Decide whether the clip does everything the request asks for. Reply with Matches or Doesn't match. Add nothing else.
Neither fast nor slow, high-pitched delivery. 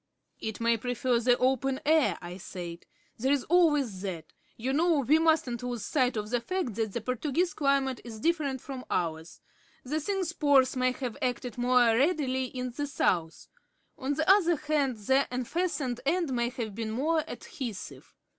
Matches